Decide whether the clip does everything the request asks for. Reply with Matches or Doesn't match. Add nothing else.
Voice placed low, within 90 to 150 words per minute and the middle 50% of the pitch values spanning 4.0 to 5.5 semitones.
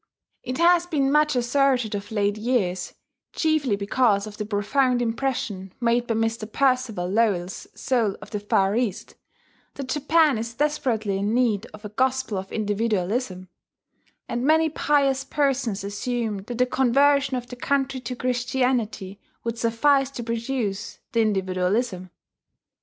Doesn't match